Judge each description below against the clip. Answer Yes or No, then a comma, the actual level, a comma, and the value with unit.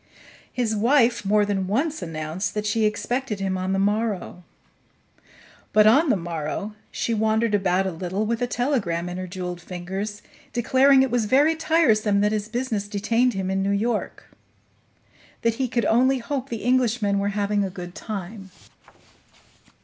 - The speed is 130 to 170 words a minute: Yes, average, 165 wpm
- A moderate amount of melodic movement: Yes, average, 3.8 semitones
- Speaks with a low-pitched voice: No, high, 210 Hz